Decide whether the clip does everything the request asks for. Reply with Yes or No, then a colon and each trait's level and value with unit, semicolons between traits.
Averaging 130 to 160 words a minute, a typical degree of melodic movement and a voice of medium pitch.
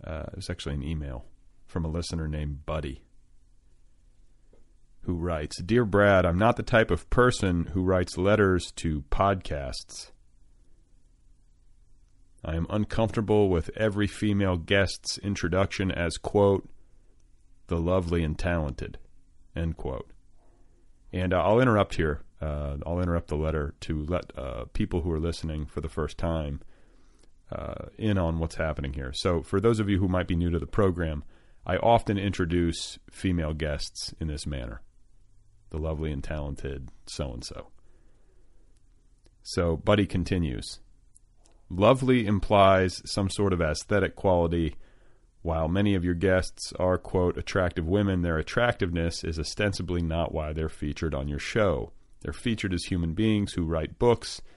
No: average, 145 wpm; average, 3.9 semitones; very low, 85 Hz